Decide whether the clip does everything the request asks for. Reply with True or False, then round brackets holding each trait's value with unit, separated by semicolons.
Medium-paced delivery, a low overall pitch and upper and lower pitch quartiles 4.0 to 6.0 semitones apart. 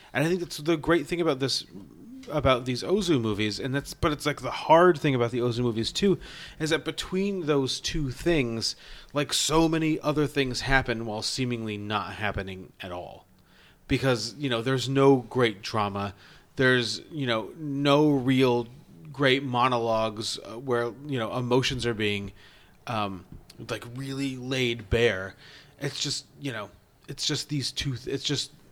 True (165 wpm; 130 Hz; 4.4 semitones)